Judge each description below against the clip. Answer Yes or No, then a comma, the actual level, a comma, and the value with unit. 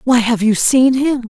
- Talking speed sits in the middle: No, fast, 230 wpm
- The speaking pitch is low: No, high, 240 Hz